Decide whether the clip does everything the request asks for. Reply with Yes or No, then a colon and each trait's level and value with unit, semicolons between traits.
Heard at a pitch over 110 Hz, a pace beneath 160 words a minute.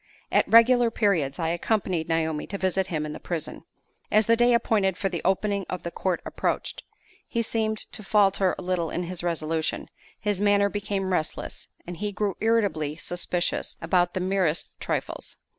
No: high, 190 Hz; average, 175 wpm